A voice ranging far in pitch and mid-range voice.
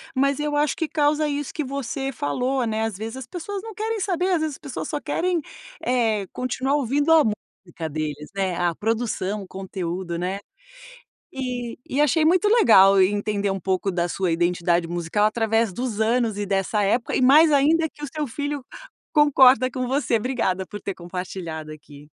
No: wide, 7.4 semitones; high, 230 Hz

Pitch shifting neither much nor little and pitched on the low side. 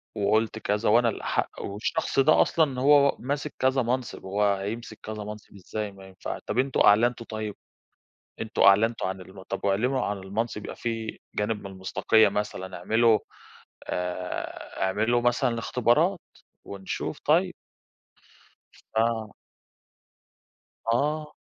Yes: average, 3.2 semitones; low, 110 Hz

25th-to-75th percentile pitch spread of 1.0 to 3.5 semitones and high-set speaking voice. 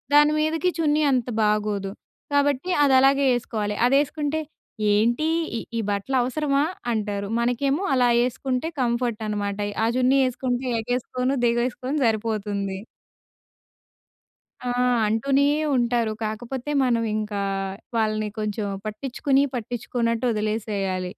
No: average, 3.9 semitones; high, 240 Hz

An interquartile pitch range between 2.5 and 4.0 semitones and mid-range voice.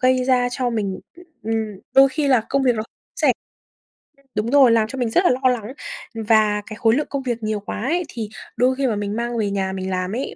No: average, 3.3 semitones; high, 235 Hz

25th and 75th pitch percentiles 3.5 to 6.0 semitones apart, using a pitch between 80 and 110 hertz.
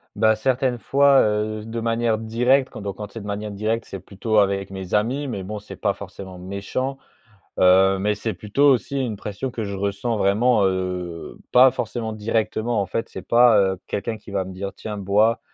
No: average, 2.9 semitones; low, 105 Hz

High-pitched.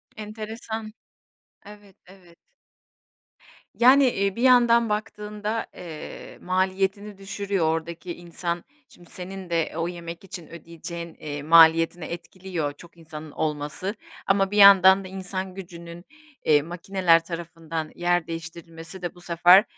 No: medium, 175 Hz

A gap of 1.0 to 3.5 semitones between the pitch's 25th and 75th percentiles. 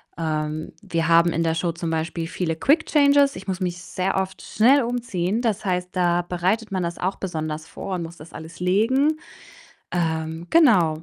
No: average, 4.0 semitones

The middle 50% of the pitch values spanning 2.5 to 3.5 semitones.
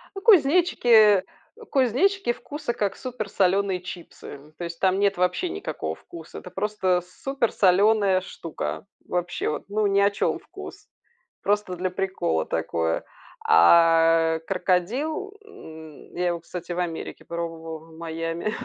No: average, 4.4 semitones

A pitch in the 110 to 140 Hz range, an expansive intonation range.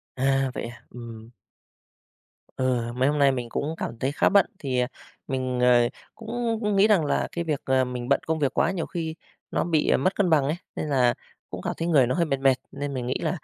No: low, 135 Hz; average, 4.3 semitones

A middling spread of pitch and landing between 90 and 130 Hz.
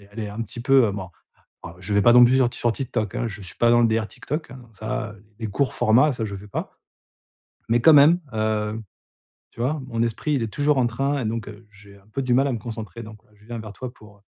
Yes: average, 3.1 semitones; low, 115 Hz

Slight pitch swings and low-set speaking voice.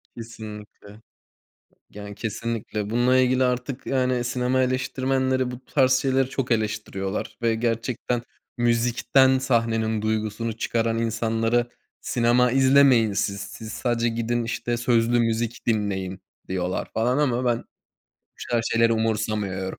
Yes: narrow, 2.3 semitones; low, 115 Hz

